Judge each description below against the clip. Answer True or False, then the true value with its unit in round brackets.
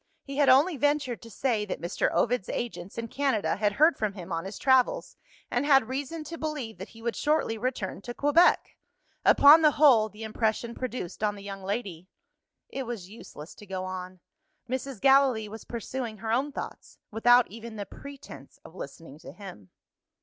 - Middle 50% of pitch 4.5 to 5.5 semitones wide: True (5.0 semitones)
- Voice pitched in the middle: False (230 Hz)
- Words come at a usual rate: True (185 wpm)